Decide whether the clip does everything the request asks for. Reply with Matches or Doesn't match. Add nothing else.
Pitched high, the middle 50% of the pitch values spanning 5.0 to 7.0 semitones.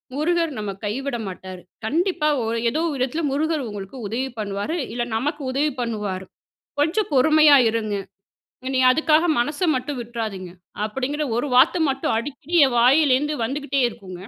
Matches